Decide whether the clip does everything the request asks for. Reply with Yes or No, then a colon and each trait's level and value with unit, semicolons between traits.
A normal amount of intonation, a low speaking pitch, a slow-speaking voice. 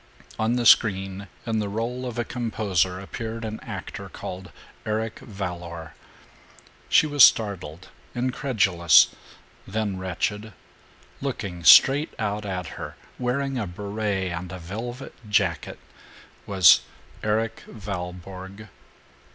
Yes: average, 3.6 semitones; low, 105 Hz; slow, 110 wpm